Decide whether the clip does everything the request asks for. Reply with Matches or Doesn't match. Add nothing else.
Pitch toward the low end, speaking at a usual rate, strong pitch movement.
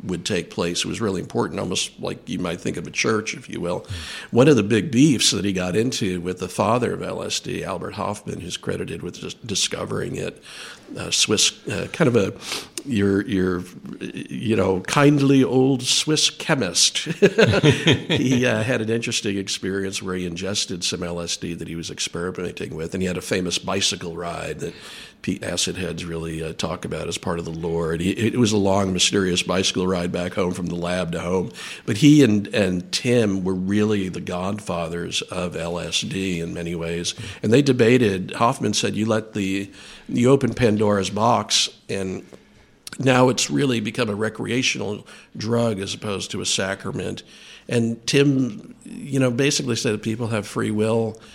Doesn't match